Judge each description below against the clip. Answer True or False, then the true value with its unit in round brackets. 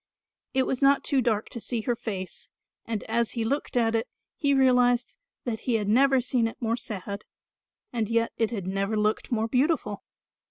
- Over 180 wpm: True (190 wpm)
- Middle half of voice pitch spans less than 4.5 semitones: True (2.6 semitones)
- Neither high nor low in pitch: False (230 Hz)